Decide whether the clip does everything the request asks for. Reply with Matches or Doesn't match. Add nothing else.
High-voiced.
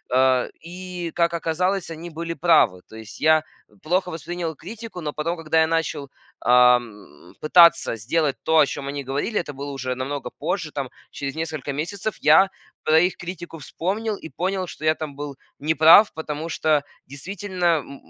Doesn't match